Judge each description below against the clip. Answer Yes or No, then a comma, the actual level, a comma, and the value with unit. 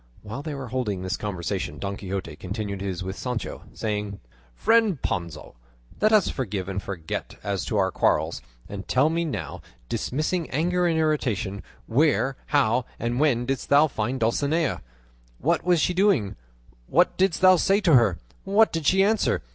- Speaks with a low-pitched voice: Yes, low, 125 Hz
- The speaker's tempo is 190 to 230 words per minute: No, average, 165 wpm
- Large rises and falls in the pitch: Yes, wide, 8.6 semitones